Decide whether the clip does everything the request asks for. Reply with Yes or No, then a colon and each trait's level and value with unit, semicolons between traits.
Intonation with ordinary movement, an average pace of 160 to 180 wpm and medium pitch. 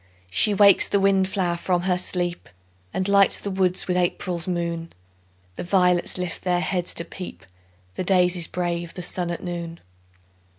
No: narrow, 1.5 semitones; average, 165 wpm; medium, 180 Hz